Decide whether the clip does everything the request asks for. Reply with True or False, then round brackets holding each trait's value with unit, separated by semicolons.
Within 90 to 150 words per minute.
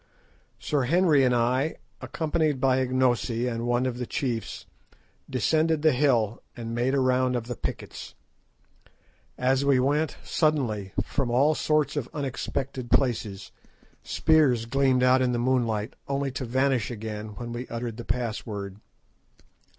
True (145 wpm)